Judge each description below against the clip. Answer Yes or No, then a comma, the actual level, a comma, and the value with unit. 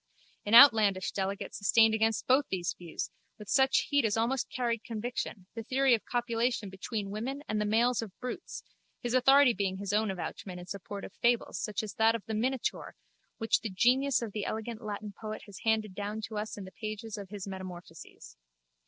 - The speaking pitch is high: Yes, high, 220 Hz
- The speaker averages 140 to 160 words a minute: No, average, 195 wpm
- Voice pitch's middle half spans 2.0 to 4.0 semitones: Yes, average, 3.0 semitones